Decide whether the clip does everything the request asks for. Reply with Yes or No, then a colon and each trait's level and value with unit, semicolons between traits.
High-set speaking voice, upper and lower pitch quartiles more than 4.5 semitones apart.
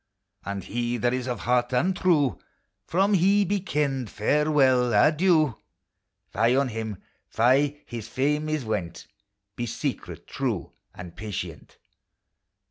No: low, 130 Hz; average, 5.1 semitones